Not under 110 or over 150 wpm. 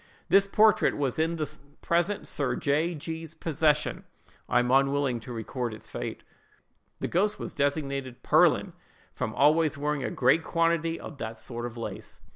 No: average, 160 wpm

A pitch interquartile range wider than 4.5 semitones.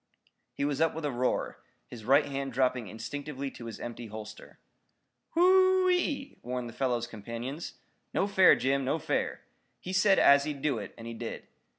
Yes: average, 5.3 semitones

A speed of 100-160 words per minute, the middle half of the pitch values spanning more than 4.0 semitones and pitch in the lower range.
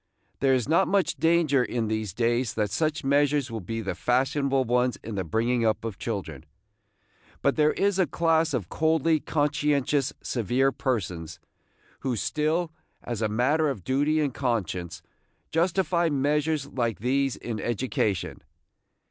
Yes: average, 150 wpm; average, 5.0 semitones; low, 130 Hz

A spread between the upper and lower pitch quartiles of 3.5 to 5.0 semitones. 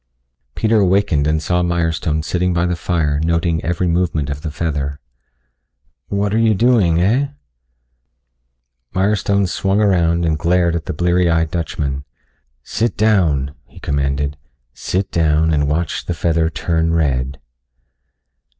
No: average, 3.0 semitones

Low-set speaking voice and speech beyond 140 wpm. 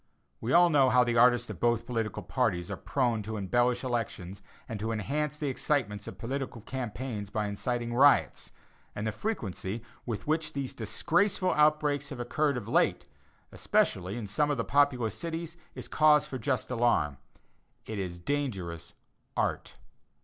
Yes: low, 120 Hz; average, 160 wpm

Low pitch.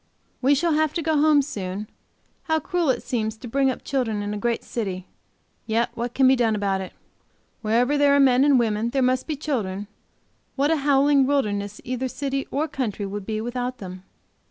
No: very high, 250 Hz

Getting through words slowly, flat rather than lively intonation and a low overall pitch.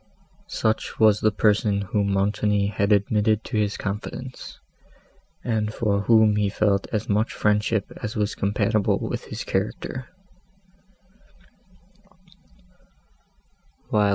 Yes: slow, 105 wpm; narrow, 1.2 semitones; low, 105 Hz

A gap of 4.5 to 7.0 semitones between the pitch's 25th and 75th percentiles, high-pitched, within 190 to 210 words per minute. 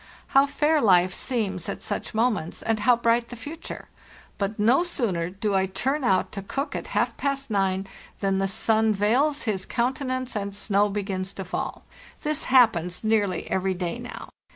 No: average, 4.8 semitones; high, 215 Hz; average, 175 wpm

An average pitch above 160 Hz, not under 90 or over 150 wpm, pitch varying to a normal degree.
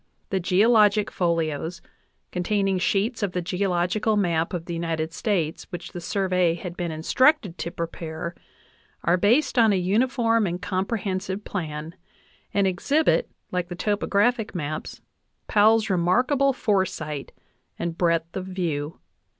Yes: medium, 185 Hz; slow, 135 wpm; average, 3.7 semitones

